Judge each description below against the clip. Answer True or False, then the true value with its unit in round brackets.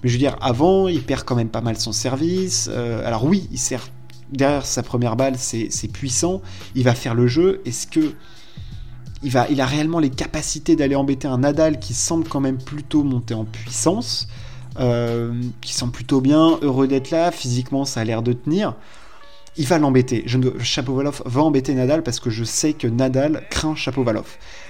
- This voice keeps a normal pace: True (195 wpm)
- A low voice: True (130 Hz)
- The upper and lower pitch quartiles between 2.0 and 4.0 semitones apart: True (3.6 semitones)